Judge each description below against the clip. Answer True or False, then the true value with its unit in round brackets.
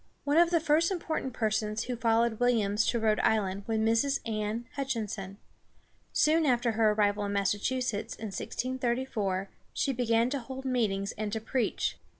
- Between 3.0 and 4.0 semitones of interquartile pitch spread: True (3.5 semitones)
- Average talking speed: True (160 wpm)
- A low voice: False (230 Hz)